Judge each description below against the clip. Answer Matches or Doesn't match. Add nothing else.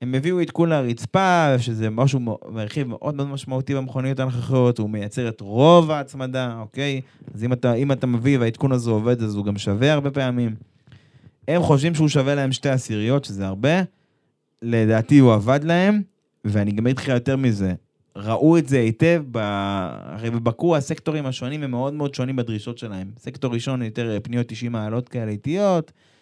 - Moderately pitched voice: Doesn't match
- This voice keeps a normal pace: Doesn't match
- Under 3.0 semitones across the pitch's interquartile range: Doesn't match